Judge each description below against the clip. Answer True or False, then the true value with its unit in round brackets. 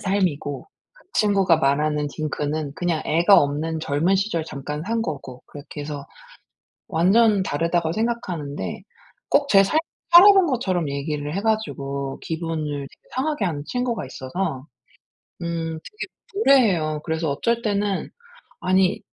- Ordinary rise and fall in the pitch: False (5.8 semitones)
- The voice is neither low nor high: True (170 Hz)